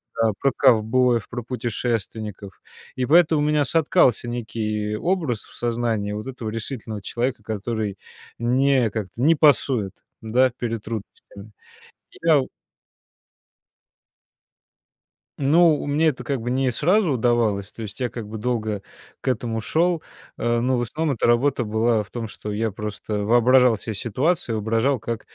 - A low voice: Yes, low, 120 Hz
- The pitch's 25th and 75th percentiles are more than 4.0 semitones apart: No, average, 3.4 semitones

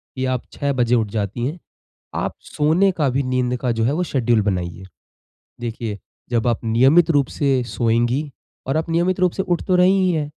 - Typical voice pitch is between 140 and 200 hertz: No, low, 130 Hz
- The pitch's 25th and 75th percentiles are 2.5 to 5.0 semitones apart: No, wide, 5.5 semitones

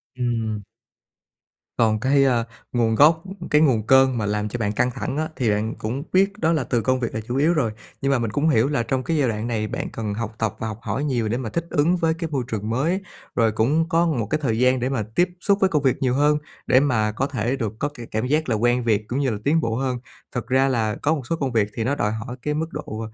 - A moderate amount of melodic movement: Yes, average, 4.6 semitones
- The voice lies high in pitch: No, low, 125 Hz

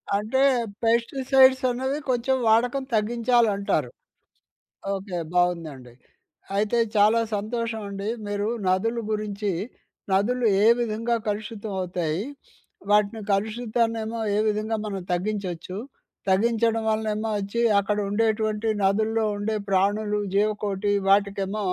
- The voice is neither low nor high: No, high, 215 Hz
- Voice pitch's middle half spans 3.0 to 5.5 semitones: No, narrow, 2.4 semitones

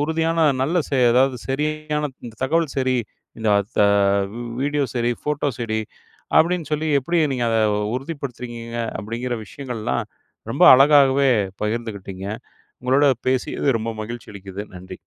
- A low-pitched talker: Yes, low, 130 Hz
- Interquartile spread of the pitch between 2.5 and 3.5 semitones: No, average, 4.5 semitones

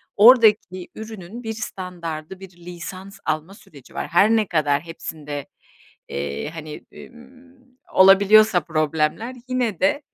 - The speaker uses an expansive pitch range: Yes, wide, 5.8 semitones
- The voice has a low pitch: No, high, 190 Hz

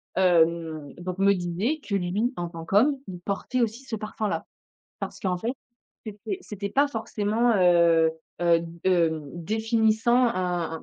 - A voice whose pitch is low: No, high, 195 Hz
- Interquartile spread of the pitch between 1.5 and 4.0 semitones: No, average, 4.4 semitones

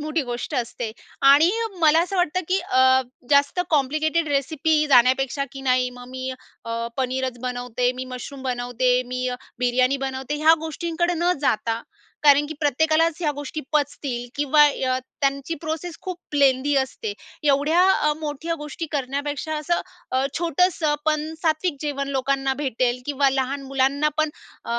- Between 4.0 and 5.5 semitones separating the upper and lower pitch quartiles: No, average, 3.2 semitones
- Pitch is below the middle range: No, very high, 285 Hz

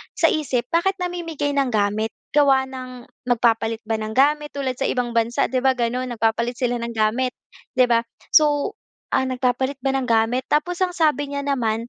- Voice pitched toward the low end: No, very high, 255 Hz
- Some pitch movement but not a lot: Yes, average, 3.5 semitones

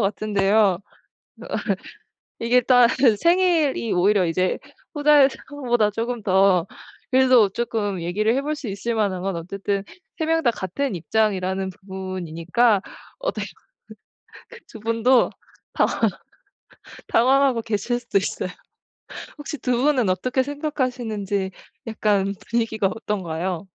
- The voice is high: Yes, high, 220 Hz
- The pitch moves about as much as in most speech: Yes, average, 4.7 semitones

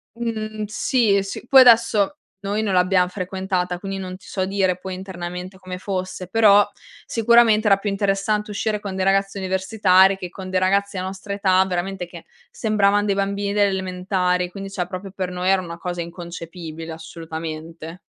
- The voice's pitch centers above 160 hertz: Yes, high, 190 Hz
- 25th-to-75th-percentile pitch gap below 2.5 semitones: Yes, narrow, 1.9 semitones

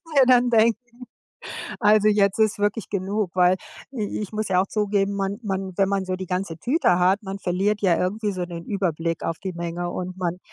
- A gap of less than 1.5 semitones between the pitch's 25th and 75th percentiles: No, narrow, 2.6 semitones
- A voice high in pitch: Yes, high, 195 Hz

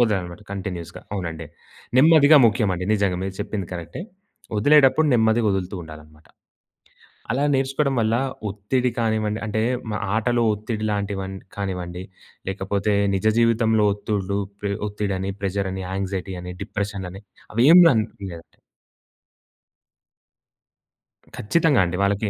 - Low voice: Yes, low, 100 Hz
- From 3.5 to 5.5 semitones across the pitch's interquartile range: No, average, 2.9 semitones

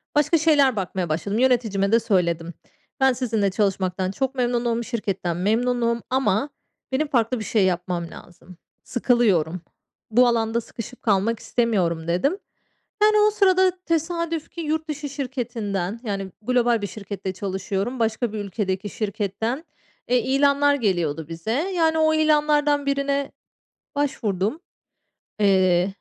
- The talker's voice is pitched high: Yes, high, 230 Hz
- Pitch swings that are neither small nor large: No, wide, 6.3 semitones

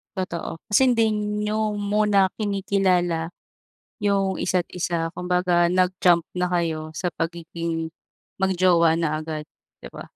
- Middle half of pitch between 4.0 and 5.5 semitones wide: No, average, 3.0 semitones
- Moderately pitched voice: Yes, medium, 180 Hz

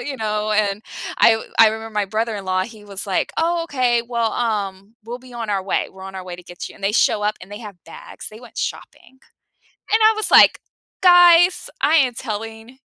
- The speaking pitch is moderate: No, high, 220 Hz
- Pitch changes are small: No, average, 3.7 semitones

